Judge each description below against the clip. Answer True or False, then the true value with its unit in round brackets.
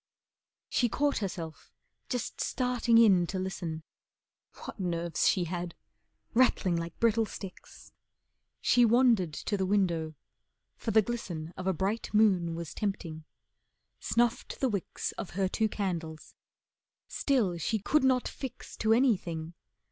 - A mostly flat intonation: False (5.2 semitones)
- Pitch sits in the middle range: False (195 Hz)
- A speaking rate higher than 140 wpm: False (135 wpm)